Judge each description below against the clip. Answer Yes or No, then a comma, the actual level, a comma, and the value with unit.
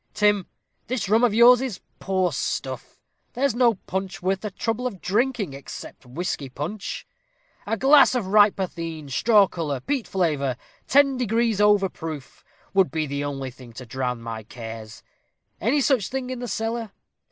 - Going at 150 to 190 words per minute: Yes, average, 165 wpm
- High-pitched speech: Yes, high, 195 Hz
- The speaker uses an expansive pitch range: Yes, wide, 8.5 semitones